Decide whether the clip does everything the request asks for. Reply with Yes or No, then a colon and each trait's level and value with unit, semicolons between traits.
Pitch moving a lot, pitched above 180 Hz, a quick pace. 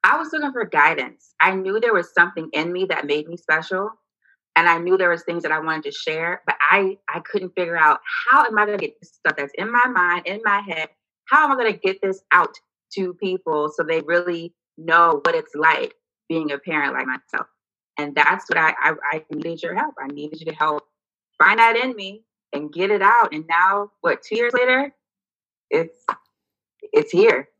Yes: wide, 6.2 semitones; high, 190 Hz; fast, 220 wpm